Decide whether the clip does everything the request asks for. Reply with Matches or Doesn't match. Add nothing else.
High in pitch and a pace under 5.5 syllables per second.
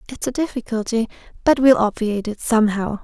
Doesn't match